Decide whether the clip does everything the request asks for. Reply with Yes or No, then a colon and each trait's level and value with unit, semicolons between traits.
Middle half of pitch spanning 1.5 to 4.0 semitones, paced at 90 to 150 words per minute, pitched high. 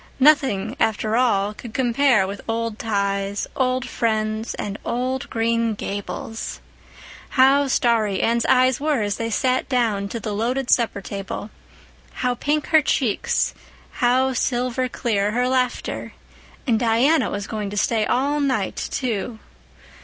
Yes: average, 3.4 semitones; average, 140 wpm; high, 230 Hz